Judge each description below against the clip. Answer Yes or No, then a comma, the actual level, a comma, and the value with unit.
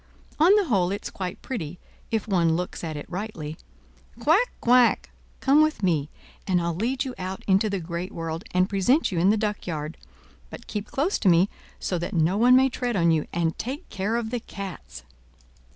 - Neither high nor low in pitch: No, high, 195 Hz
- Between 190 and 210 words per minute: Yes, average, 195 wpm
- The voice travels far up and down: Yes, wide, 5.8 semitones